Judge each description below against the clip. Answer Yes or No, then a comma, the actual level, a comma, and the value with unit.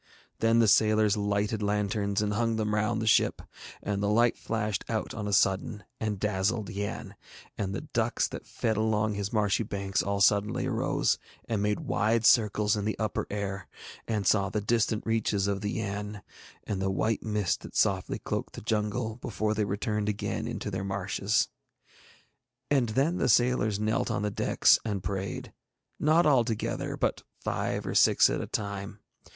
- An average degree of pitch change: No, narrow, 1.6 semitones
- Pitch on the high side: No, low, 105 Hz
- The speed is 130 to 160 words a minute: No, average, 175 wpm